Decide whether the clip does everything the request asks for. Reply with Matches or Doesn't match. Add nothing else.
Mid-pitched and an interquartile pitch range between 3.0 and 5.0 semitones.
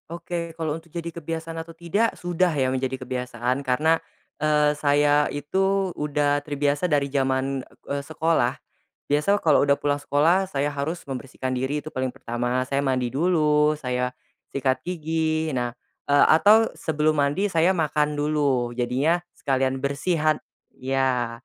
Matches